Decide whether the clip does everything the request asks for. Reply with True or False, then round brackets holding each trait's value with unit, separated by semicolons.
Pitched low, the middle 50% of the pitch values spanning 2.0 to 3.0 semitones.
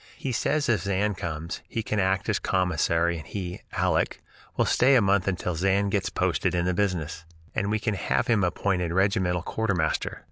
True (95 Hz; 2.7 semitones)